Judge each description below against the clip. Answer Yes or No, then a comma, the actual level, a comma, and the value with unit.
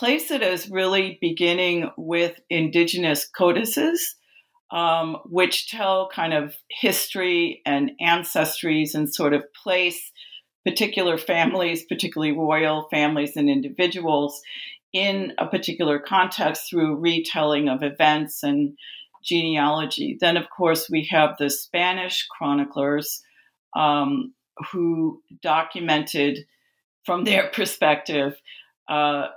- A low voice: No, medium, 165 Hz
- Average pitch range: Yes, average, 3.3 semitones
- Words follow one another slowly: Yes, slow, 105 wpm